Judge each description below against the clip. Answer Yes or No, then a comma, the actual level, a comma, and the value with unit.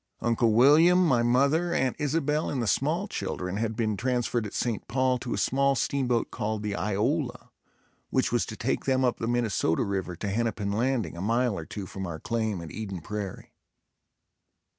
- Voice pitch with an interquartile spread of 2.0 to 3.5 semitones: No, average, 4.3 semitones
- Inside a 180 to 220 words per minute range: Yes, average, 185 wpm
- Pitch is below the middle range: Yes, low, 115 Hz